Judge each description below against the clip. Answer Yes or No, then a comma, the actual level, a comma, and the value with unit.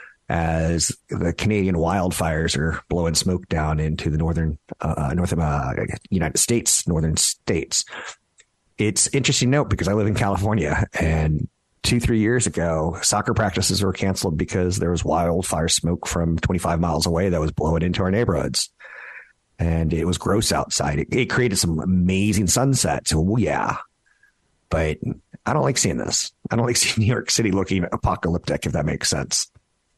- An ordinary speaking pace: Yes, average, 170 wpm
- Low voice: Yes, very low, 90 Hz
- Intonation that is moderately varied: Yes, average, 4.2 semitones